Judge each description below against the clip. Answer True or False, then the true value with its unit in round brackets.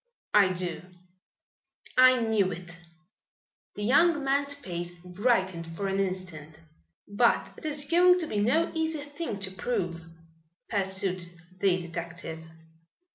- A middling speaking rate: False (125 wpm)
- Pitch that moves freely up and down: True (7.5 semitones)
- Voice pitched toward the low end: False (195 Hz)